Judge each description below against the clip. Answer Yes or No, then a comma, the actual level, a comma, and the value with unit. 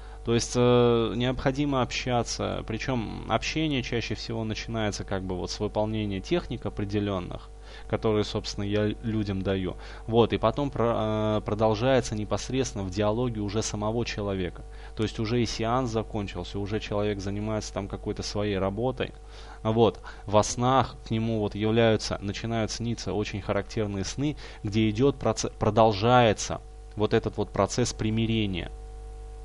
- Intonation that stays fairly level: Yes, narrow, 2.1 semitones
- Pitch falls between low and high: No, low, 110 Hz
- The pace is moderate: Yes, average, 135 wpm